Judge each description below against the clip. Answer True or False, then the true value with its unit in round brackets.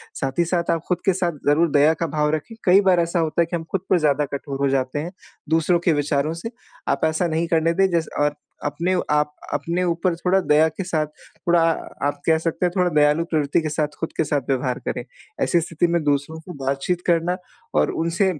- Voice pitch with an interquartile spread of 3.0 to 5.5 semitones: False (2.6 semitones)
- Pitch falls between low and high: True (165 Hz)